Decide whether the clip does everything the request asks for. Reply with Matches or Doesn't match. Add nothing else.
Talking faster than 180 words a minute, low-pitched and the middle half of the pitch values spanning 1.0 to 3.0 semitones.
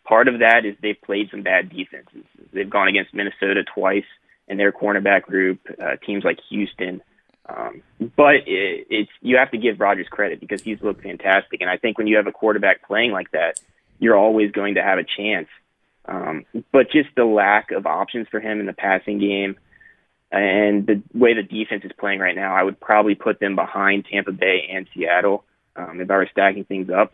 Matches